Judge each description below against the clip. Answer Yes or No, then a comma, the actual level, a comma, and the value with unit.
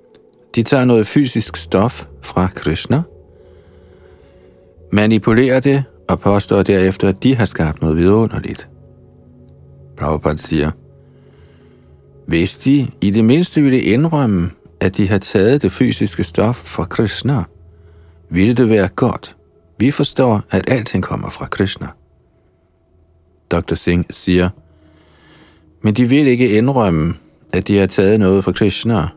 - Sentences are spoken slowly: Yes, slow, 130 wpm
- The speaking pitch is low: Yes, very low, 95 Hz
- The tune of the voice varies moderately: No, wide, 5.7 semitones